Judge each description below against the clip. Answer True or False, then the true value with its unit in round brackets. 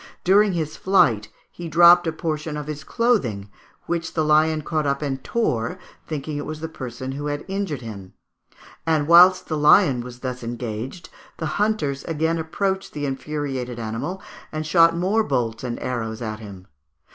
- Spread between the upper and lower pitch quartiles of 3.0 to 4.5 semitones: False (5.1 semitones)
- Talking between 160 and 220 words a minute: True (170 wpm)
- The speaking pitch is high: False (150 Hz)